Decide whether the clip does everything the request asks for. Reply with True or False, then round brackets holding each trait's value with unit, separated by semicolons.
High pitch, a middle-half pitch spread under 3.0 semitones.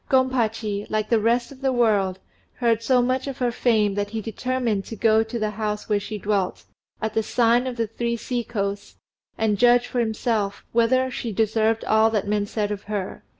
True (225 Hz; 2.5 semitones)